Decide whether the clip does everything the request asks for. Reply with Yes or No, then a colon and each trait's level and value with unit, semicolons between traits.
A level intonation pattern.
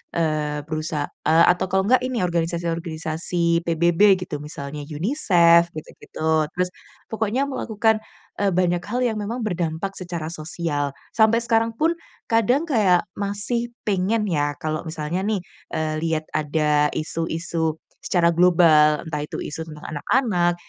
No: average, 4.7 semitones